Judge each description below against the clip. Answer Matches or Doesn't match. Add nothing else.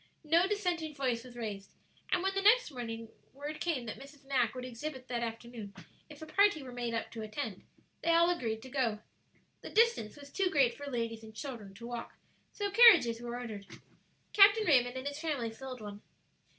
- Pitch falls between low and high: Doesn't match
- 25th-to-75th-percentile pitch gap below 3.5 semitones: Doesn't match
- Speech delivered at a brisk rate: Doesn't match